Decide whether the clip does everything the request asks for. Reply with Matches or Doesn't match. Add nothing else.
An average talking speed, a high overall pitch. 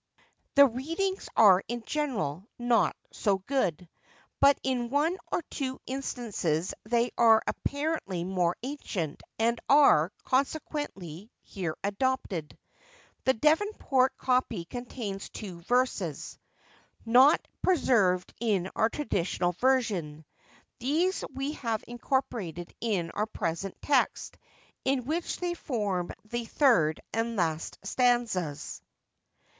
Doesn't match